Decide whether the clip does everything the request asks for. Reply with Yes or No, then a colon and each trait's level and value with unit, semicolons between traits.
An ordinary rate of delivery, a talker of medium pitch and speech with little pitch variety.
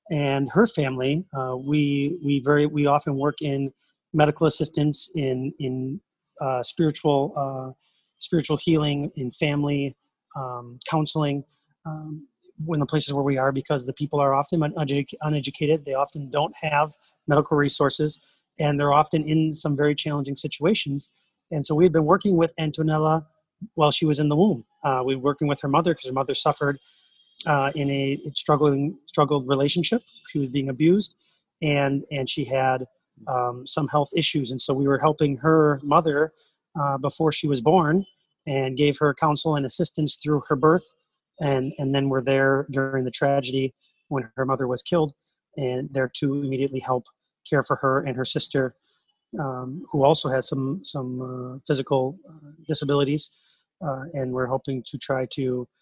Yes: average, 165 wpm; medium, 145 Hz; narrow, 2.2 semitones